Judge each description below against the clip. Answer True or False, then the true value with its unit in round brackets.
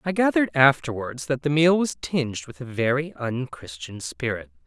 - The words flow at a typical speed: True (165 wpm)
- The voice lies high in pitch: False (135 Hz)